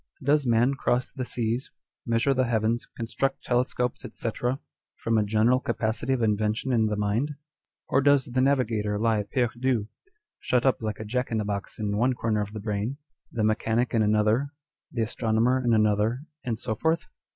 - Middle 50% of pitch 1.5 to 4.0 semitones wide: Yes, average, 2.8 semitones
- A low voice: Yes, low, 115 Hz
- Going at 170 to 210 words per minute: Yes, average, 175 wpm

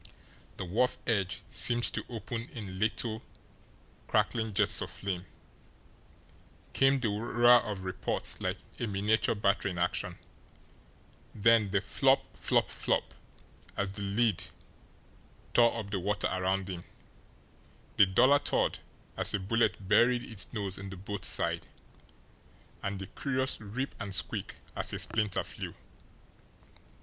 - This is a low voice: Yes, low, 105 Hz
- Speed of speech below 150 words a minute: Yes, slow, 135 wpm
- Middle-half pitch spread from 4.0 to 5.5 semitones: No, average, 3.3 semitones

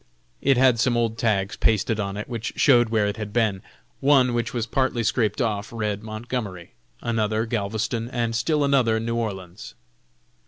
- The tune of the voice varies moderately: No, narrow, 2.1 semitones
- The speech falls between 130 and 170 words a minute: Yes, average, 165 wpm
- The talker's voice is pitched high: No, low, 115 Hz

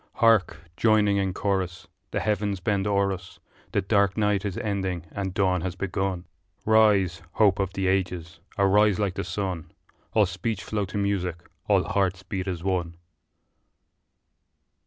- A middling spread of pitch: No, narrow, 1.9 semitones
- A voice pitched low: Yes, very low, 95 Hz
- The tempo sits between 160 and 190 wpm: No, average, 150 wpm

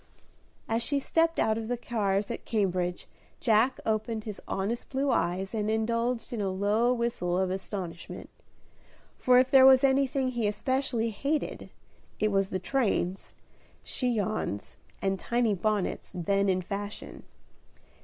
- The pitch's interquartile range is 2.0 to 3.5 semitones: No, average, 4.0 semitones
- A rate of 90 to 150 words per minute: Yes, average, 140 wpm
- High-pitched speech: Yes, high, 220 Hz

